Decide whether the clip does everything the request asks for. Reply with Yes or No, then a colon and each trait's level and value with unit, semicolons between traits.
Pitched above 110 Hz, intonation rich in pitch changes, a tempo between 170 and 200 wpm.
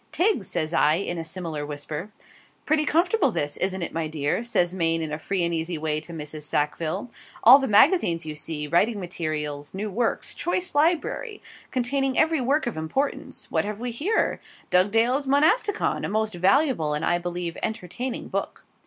Yes: medium, 185 Hz; wide, 8.7 semitones; average, 175 wpm